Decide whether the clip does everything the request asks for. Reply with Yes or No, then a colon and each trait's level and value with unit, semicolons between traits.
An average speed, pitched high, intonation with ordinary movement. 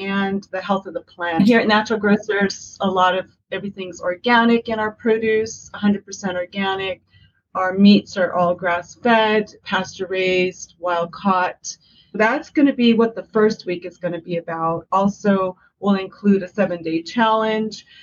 Yes: average, 155 wpm; high, 195 Hz; average, 3.1 semitones